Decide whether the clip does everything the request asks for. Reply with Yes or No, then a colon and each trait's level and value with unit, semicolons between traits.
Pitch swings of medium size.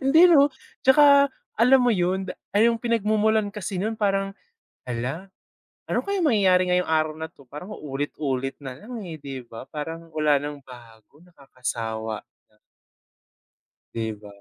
No: wide, 8.2 semitones